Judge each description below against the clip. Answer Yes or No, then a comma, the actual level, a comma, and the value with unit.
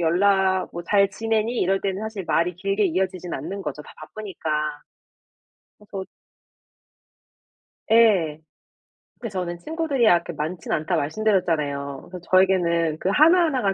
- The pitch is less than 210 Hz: Yes, high, 190 Hz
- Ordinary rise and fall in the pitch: Yes, average, 3.9 semitones